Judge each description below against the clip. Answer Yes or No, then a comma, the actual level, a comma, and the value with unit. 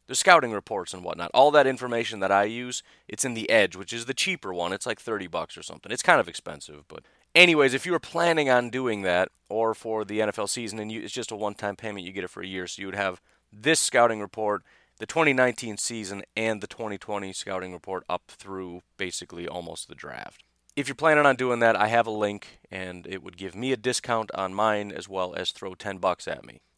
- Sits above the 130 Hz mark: No, low, 105 Hz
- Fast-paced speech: Yes, fast, 235 wpm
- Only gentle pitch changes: No, average, 4.3 semitones